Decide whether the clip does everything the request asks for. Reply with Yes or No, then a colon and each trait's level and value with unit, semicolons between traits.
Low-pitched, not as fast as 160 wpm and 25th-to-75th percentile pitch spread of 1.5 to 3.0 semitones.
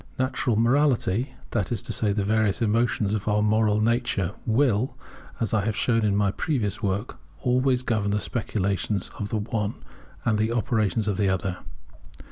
No: low, 110 Hz; average, 170 wpm; narrow, 2.5 semitones